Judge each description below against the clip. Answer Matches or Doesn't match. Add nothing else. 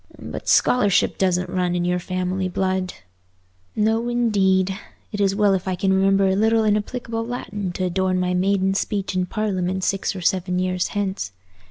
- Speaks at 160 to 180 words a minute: Matches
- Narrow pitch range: Matches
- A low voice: Doesn't match